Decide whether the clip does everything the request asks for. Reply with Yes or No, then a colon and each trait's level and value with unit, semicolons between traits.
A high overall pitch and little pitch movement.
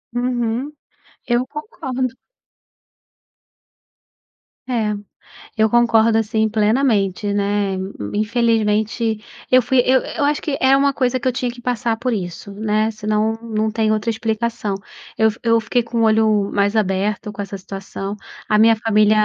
Yes: high, 225 Hz; narrow, 2.3 semitones